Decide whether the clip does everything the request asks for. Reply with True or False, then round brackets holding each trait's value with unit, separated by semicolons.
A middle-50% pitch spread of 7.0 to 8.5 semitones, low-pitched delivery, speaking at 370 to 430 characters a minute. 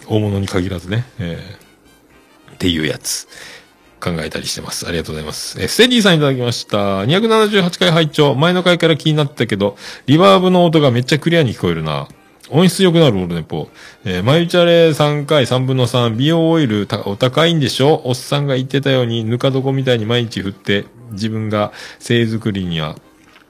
True (7.3 semitones; 130 Hz; 375 characters per minute)